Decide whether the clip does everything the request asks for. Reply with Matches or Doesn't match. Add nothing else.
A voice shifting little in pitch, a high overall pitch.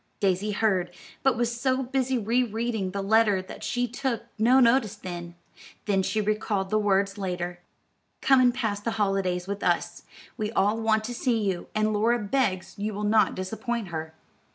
Doesn't match